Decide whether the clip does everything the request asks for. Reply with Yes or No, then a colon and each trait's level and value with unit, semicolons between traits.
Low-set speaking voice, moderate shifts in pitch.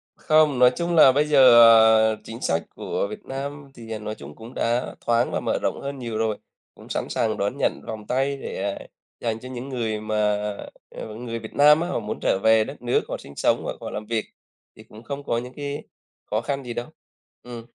Yes: low, 120 Hz; average, 4.0 semitones